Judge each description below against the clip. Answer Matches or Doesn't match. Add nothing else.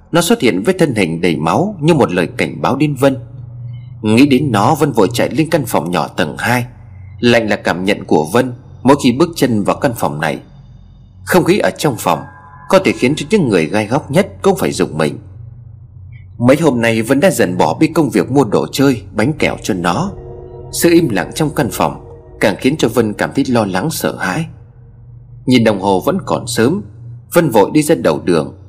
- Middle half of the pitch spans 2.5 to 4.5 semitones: Doesn't match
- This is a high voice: Doesn't match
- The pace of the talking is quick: Doesn't match